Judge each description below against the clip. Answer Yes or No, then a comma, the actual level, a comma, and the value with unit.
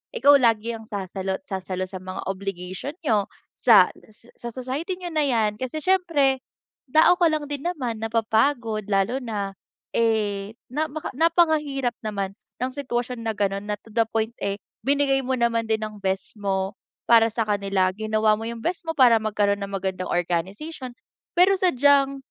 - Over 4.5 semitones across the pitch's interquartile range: Yes, wide, 5.5 semitones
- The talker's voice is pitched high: Yes, high, 225 Hz